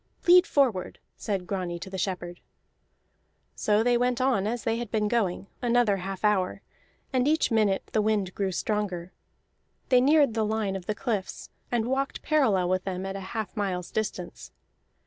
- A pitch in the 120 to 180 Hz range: No, high, 210 Hz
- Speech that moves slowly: No, average, 170 wpm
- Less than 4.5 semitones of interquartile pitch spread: Yes, average, 4.1 semitones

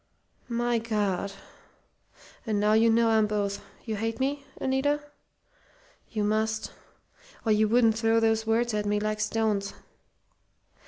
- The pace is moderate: No, slow, 130 wpm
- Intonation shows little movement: Yes, narrow, 1.5 semitones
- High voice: Yes, high, 220 Hz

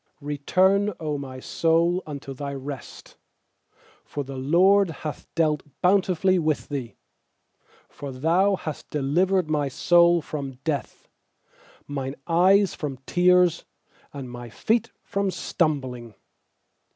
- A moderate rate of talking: No, slow, 115 wpm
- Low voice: No, medium, 155 Hz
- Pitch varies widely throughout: No, average, 4.5 semitones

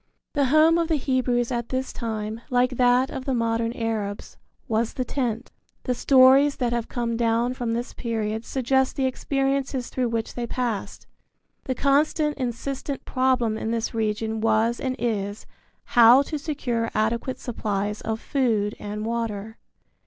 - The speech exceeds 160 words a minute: No, average, 155 wpm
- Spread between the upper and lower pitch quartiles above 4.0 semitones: No, average, 2.7 semitones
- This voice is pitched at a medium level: No, high, 240 Hz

